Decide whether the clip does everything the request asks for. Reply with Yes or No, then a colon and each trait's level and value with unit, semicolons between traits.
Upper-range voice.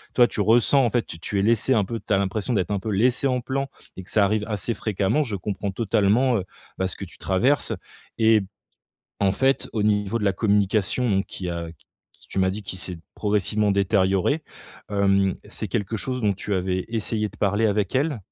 No: low, 105 Hz